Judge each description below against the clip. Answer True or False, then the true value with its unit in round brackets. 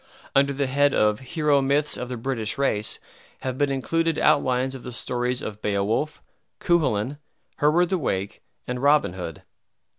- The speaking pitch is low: True (130 Hz)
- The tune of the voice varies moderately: True (4.1 semitones)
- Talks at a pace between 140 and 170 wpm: True (155 wpm)